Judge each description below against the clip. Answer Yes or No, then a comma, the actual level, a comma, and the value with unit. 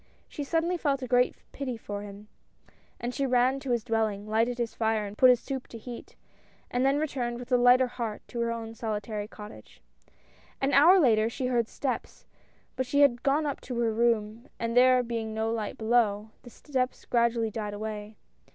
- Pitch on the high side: Yes, high, 240 Hz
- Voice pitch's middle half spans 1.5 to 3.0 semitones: Yes, narrow, 2.6 semitones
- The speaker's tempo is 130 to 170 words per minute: No, average, 195 wpm